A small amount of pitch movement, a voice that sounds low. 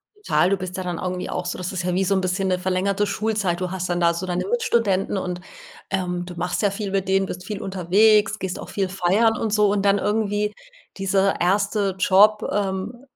No: narrow, 2.2 semitones; high, 190 Hz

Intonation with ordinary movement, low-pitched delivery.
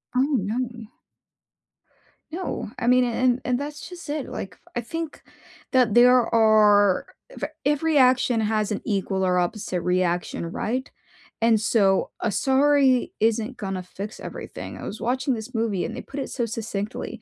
No: average, 3.9 semitones; high, 230 Hz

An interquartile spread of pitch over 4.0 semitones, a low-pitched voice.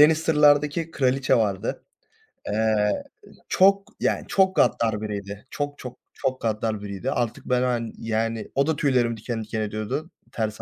Yes: average, 5.0 semitones; low, 120 Hz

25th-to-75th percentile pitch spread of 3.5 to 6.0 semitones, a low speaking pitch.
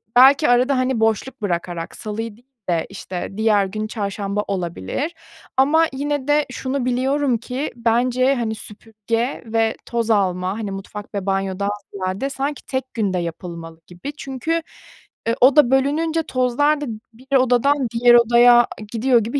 No: average, 4.7 semitones; high, 235 Hz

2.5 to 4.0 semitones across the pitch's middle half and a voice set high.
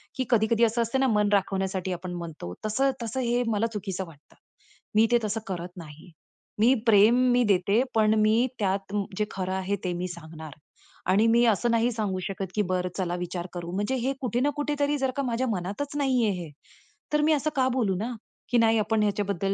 No: average, 4.4 semitones; high, 210 Hz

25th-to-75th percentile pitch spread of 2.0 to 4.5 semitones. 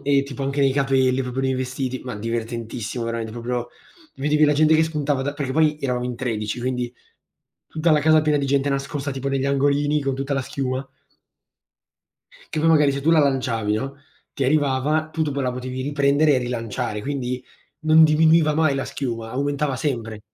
Yes: average, 2.7 semitones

